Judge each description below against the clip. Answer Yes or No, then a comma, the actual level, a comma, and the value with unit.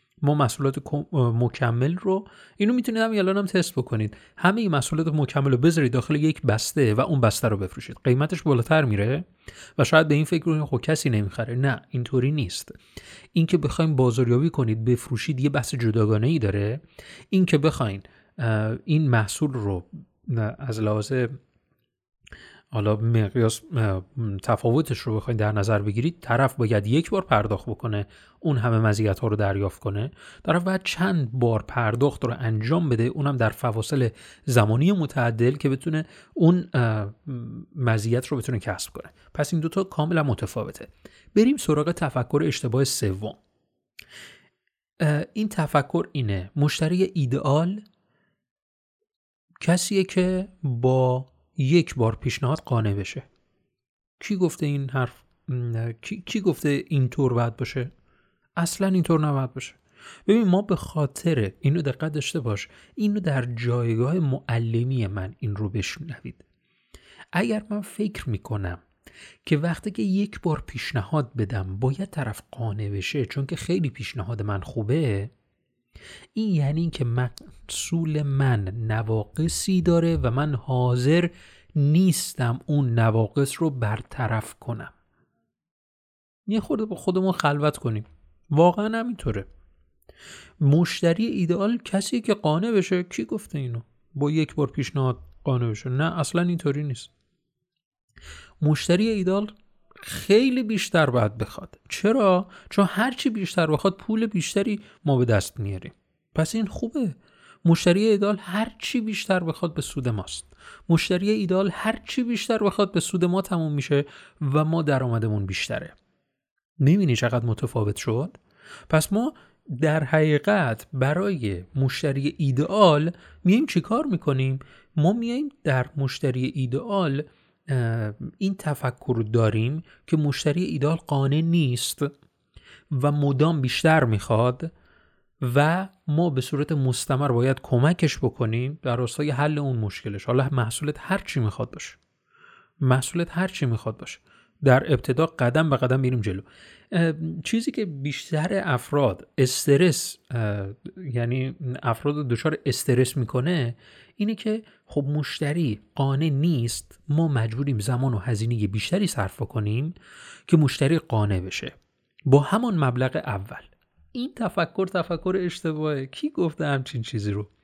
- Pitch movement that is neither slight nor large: No, wide, 6.2 semitones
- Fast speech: No, average, 130 wpm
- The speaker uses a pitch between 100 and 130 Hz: No, medium, 140 Hz